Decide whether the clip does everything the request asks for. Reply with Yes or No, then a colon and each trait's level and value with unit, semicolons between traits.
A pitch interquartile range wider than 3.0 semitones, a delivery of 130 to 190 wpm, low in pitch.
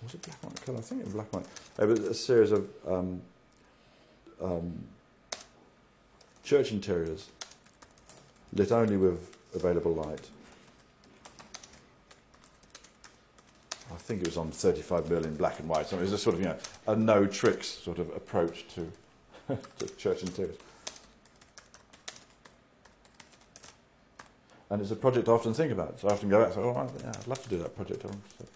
Yes: average, 3.5 semitones; average, 170 wpm; low, 100 Hz